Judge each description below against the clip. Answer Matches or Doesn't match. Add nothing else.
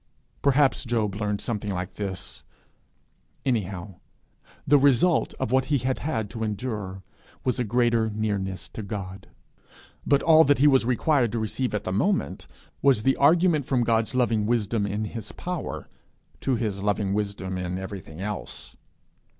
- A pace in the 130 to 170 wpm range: Matches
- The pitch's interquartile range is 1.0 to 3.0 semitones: Doesn't match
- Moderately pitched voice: Doesn't match